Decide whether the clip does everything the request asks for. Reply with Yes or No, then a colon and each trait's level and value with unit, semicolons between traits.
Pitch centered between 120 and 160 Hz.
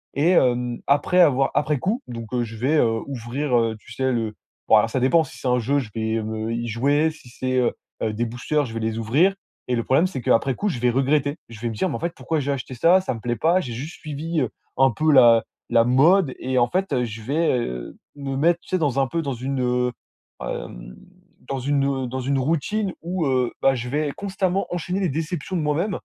Yes: low, 135 Hz